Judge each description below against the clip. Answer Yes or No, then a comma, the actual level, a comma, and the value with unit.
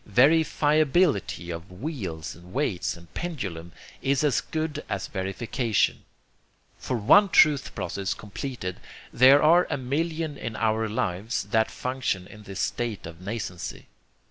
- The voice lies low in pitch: Yes, low, 115 Hz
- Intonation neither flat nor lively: No, wide, 7.5 semitones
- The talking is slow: Yes, slow, 130 wpm